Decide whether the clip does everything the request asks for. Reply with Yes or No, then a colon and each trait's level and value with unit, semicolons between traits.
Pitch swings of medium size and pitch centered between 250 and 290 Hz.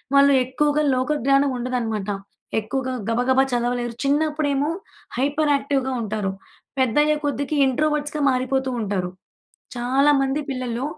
Yes: average, 3.0 semitones; very high, 265 Hz